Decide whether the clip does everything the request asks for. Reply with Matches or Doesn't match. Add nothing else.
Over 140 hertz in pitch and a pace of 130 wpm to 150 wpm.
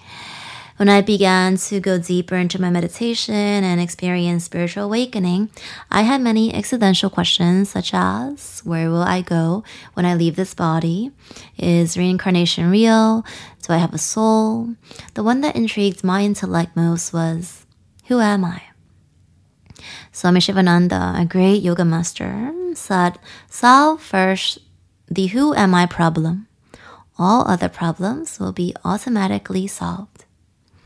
Matches